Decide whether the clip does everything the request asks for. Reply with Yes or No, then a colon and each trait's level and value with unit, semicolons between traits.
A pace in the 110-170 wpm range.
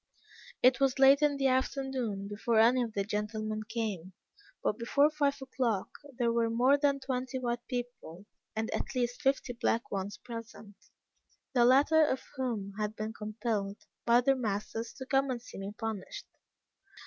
Yes: average, 160 wpm